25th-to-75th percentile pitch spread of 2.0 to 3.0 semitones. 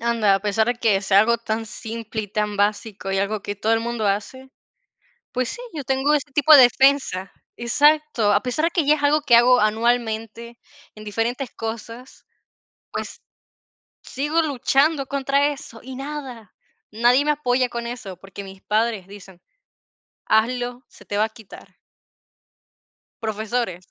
No: average, 3.8 semitones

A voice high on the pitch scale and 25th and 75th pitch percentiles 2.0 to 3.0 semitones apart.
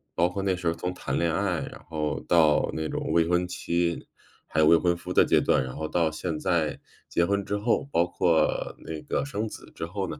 No: very low, 85 Hz; narrow, 2.4 semitones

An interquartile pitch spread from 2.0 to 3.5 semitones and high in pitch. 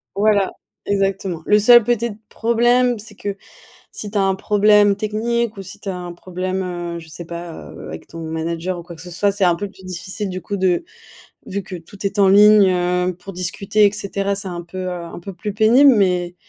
Yes: average, 2.7 semitones; high, 195 Hz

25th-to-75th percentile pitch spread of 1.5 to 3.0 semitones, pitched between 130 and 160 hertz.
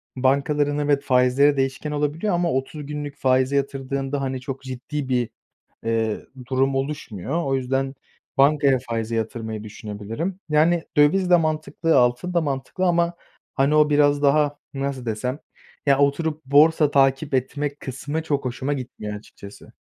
Yes: narrow, 2.5 semitones; medium, 140 Hz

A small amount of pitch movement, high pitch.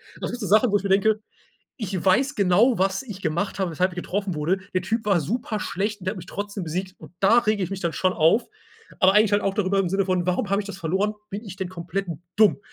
Yes: narrow, 2.2 semitones; high, 195 Hz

